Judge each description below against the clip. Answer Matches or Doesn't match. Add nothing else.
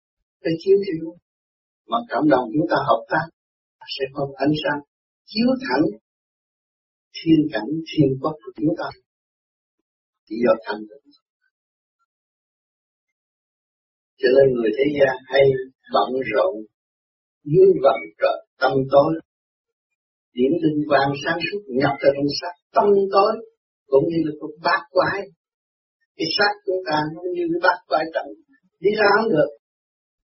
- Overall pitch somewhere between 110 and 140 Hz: Doesn't match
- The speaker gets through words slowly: Matches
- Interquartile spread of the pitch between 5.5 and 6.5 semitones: Doesn't match